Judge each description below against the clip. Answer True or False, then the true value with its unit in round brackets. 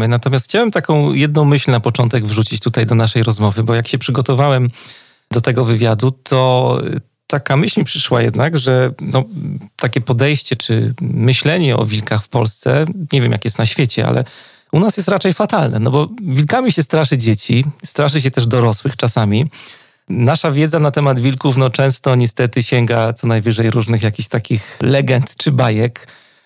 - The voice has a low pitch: True (130 Hz)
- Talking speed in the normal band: False (170 wpm)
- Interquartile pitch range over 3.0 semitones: True (3.8 semitones)